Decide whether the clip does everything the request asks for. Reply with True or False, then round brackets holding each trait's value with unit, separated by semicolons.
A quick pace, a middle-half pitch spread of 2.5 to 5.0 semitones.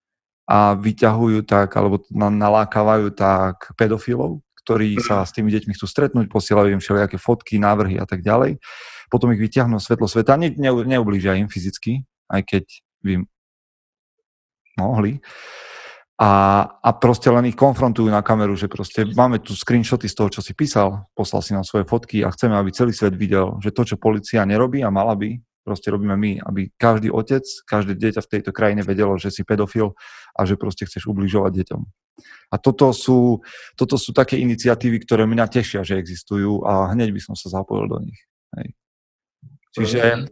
True (170 wpm; 2.9 semitones)